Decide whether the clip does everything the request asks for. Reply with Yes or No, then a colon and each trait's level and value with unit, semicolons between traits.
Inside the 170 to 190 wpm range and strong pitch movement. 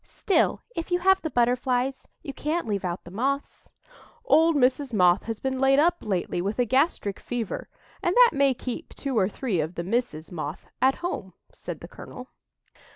Yes: average, 185 wpm; wide, 6.4 semitones